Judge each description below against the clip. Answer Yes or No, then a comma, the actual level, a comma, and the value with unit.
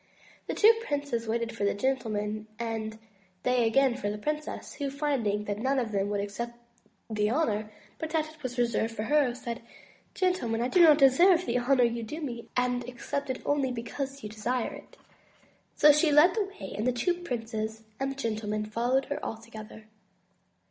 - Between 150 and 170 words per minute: No, average, 190 wpm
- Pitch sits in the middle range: No, high, 240 Hz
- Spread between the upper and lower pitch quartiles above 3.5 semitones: Yes, average, 4.3 semitones